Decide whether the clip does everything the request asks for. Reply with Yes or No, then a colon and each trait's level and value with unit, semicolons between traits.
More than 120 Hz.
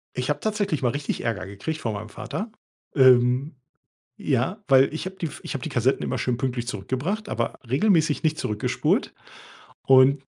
Yes: low, 135 Hz